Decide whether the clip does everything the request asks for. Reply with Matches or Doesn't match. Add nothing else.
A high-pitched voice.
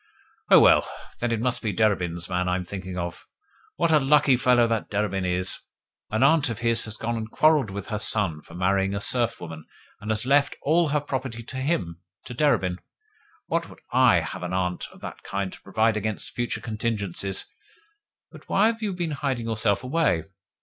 Doesn't match